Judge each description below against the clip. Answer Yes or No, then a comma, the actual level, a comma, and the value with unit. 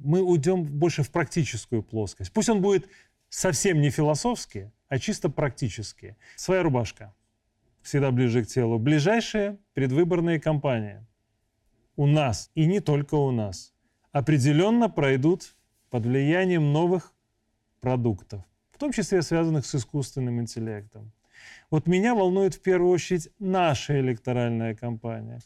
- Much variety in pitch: Yes, wide, 7.3 semitones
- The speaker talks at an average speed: Yes, average, 125 wpm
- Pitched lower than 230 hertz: Yes, medium, 140 Hz